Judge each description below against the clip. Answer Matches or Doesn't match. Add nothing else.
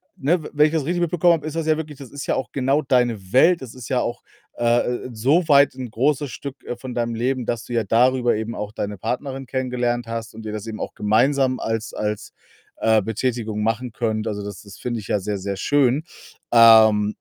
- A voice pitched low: Matches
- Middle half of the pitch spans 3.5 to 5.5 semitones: Matches